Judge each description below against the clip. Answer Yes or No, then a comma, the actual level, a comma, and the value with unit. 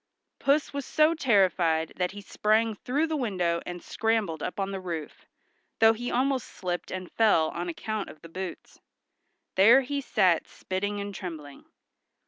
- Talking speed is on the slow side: No, average, 155 wpm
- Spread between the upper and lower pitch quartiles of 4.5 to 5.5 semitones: Yes, average, 4.8 semitones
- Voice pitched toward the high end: Yes, high, 200 Hz